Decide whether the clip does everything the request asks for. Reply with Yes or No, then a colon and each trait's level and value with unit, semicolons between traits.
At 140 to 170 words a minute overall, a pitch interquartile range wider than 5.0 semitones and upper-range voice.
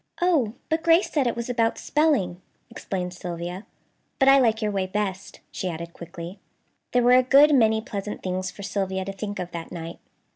No: average, 190 wpm; wide, 5.5 semitones; high, 205 Hz